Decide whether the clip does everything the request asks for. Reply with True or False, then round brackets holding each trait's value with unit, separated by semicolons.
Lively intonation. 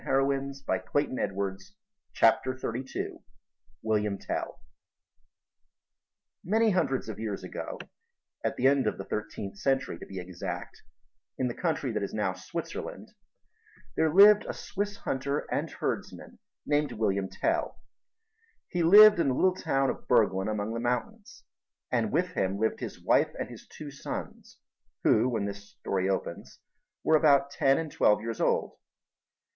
True (6.2 semitones)